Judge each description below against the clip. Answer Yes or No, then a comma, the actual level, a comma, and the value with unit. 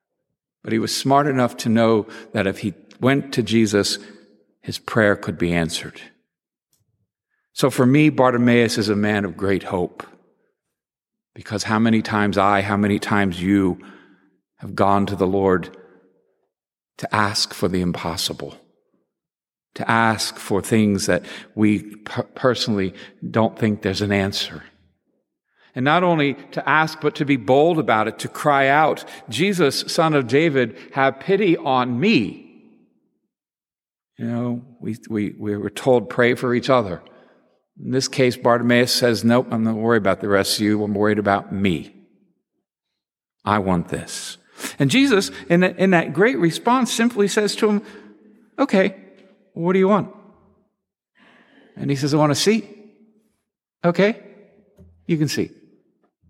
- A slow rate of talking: No, average, 150 wpm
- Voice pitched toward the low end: Yes, low, 120 Hz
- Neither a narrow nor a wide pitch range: No, wide, 6.8 semitones